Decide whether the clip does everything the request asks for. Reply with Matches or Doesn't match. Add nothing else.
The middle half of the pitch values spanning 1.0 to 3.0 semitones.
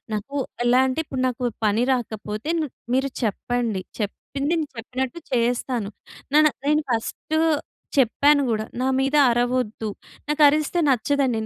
Doesn't match